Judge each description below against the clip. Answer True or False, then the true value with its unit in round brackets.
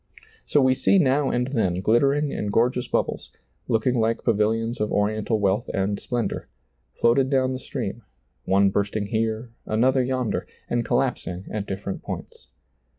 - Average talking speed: True (155 wpm)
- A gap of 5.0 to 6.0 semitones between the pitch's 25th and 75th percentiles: False (3.9 semitones)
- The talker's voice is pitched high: False (115 Hz)